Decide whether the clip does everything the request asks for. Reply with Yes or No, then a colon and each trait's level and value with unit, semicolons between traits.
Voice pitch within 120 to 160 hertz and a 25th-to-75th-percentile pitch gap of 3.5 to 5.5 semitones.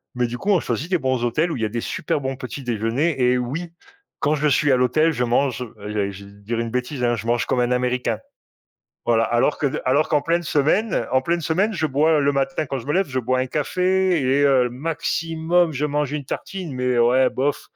Yes: low, 135 Hz; average, 4.2 semitones